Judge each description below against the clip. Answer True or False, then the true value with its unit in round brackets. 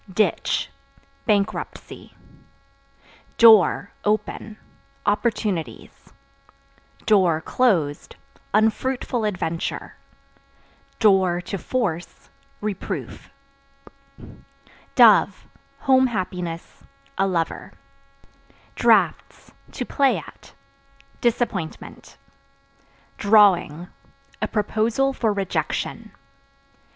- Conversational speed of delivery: False (60 wpm)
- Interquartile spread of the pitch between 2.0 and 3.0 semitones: False (3.9 semitones)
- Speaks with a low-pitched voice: False (205 Hz)